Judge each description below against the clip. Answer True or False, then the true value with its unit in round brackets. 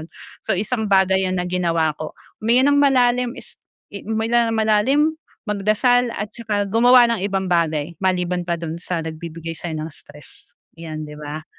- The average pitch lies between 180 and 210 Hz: True (190 Hz)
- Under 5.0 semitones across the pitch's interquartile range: False (5.4 semitones)